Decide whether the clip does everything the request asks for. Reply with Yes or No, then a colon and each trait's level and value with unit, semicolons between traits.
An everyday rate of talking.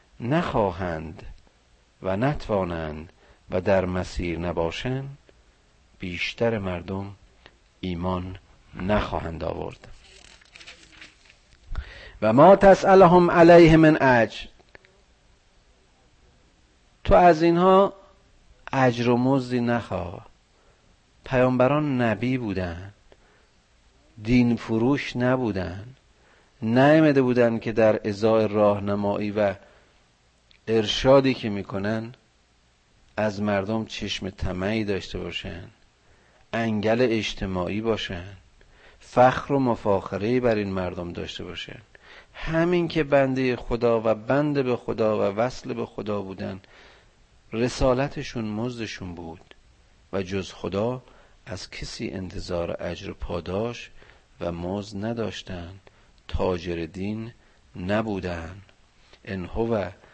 No: slow, 90 wpm